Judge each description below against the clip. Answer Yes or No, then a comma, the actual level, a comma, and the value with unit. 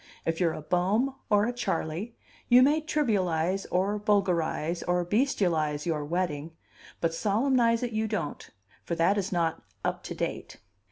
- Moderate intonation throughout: Yes, average, 5.0 semitones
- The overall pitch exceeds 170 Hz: Yes, medium, 185 Hz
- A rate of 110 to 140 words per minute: No, average, 155 wpm